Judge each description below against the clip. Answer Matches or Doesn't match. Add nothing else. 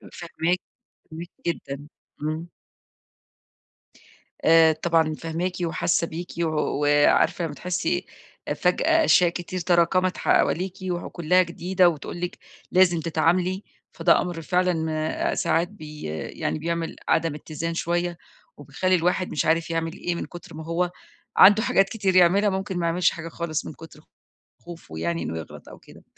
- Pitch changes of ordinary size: Doesn't match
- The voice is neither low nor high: Matches